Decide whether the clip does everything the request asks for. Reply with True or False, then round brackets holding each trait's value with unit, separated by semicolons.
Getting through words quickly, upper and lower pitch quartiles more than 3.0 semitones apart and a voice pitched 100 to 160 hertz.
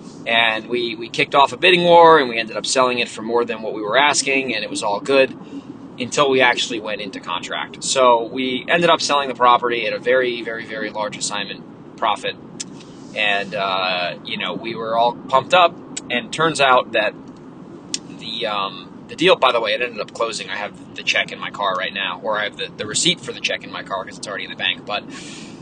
True (235 wpm; 3.7 semitones; 125 Hz)